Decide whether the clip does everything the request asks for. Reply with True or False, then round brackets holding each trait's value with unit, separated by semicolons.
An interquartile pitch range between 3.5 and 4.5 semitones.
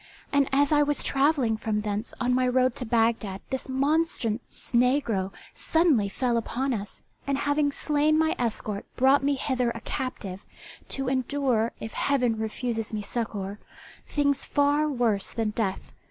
True (4.2 semitones)